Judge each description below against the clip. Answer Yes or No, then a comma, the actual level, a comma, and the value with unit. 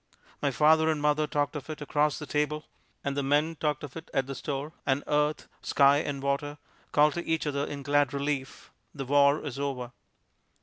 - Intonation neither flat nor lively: No, narrow, 1.3 semitones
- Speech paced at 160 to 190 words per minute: No, average, 200 wpm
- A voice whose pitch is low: No, medium, 145 Hz